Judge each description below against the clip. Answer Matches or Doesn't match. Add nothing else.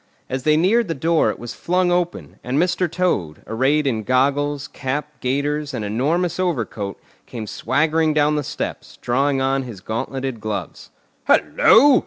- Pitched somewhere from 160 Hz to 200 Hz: Doesn't match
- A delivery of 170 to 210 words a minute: Doesn't match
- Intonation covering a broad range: Doesn't match